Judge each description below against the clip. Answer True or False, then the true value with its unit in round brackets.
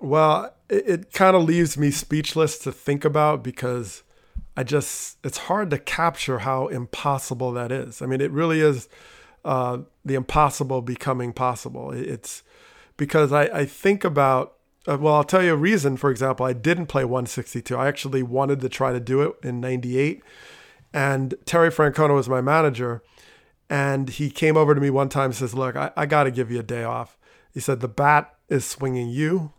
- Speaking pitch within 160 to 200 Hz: False (140 Hz)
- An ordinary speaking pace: True (190 wpm)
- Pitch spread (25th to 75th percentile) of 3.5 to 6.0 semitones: False (2.9 semitones)